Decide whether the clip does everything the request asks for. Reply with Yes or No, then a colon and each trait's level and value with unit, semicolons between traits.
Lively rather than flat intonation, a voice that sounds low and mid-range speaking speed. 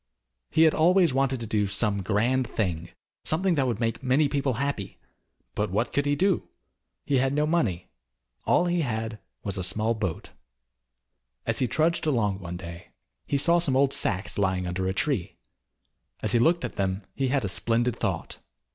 Yes: wide, 6.1 semitones; low, 120 Hz; average, 180 wpm